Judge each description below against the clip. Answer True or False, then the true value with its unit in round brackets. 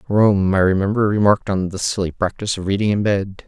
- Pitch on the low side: True (100 Hz)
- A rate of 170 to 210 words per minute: True (205 wpm)